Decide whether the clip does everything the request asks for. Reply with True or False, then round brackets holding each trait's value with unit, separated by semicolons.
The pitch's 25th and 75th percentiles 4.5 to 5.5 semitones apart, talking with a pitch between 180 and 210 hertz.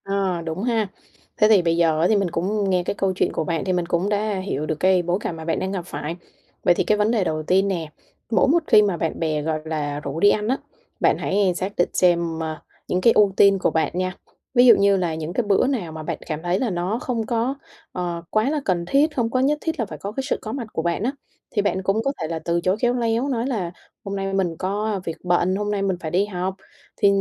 False (3.8 semitones; 190 Hz)